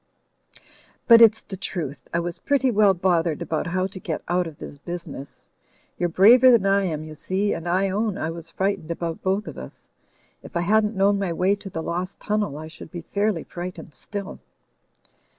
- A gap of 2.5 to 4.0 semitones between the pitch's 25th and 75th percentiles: Yes, average, 3.3 semitones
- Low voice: No, medium, 185 Hz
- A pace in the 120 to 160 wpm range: No, average, 195 wpm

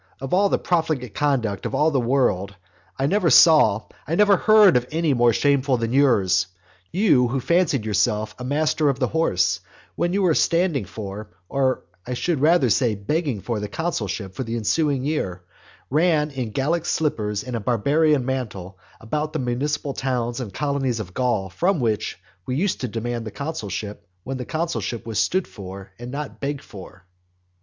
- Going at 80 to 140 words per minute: No, average, 180 wpm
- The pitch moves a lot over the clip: Yes, wide, 5.9 semitones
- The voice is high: No, low, 130 Hz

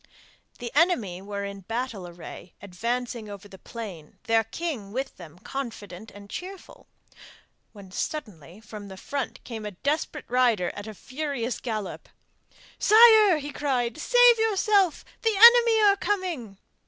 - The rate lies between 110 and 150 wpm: Yes, average, 140 wpm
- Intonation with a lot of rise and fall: Yes, wide, 8.5 semitones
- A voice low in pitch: No, high, 235 Hz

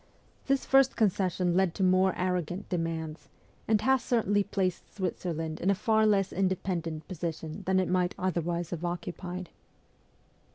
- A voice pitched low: No, medium, 185 Hz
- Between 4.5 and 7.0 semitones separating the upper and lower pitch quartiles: No, narrow, 2.4 semitones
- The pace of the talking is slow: No, average, 150 wpm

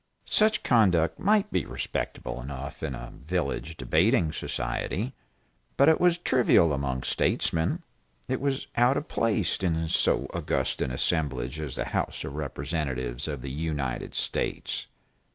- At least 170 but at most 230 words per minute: No, average, 140 wpm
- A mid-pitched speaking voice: No, very low, 80 Hz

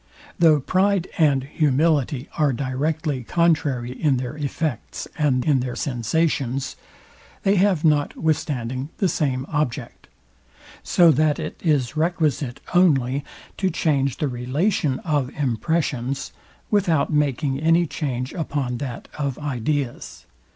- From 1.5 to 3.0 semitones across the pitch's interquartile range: No, average, 3.7 semitones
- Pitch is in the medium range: Yes, medium, 145 Hz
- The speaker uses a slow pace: Yes, slow, 115 wpm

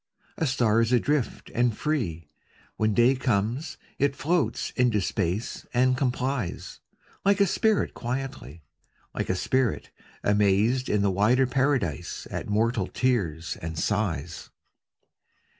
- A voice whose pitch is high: No, low, 120 Hz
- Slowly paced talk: Yes, slow, 125 wpm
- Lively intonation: No, average, 4.7 semitones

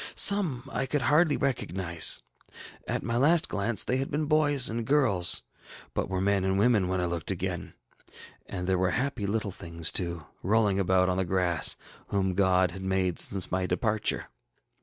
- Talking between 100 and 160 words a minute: No, average, 180 wpm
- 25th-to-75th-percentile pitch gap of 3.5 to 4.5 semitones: No, average, 5.3 semitones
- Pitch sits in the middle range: No, very low, 95 Hz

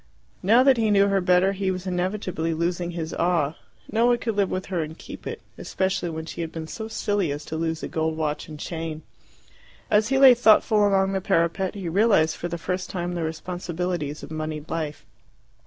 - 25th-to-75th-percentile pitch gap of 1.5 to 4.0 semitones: Yes, average, 3.5 semitones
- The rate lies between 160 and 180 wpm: No, fast, 205 wpm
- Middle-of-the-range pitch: Yes, medium, 180 Hz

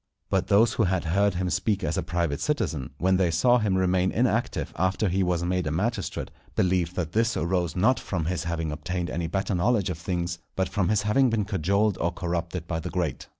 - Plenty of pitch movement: No, average, 2.8 semitones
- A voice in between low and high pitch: No, very low, 90 Hz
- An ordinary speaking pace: No, fast, 215 wpm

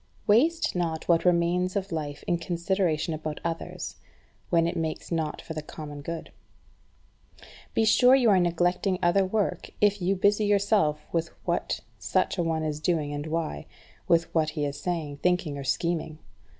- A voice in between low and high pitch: Yes, medium, 170 Hz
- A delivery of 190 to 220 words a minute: No, average, 170 wpm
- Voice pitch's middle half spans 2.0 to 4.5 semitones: Yes, average, 3.2 semitones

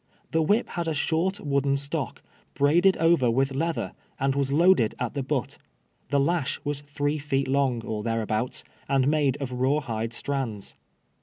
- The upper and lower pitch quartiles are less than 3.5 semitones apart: Yes, average, 3.1 semitones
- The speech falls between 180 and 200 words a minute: No, average, 165 wpm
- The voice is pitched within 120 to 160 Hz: Yes, medium, 140 Hz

